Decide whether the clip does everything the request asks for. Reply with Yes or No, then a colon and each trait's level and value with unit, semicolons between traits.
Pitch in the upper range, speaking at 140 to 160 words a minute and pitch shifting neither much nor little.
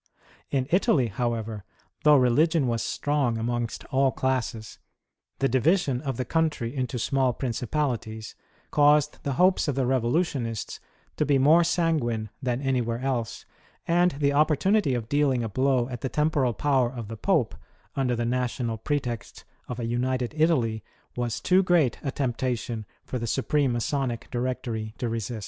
No: low, 130 Hz; average, 155 wpm; average, 3.6 semitones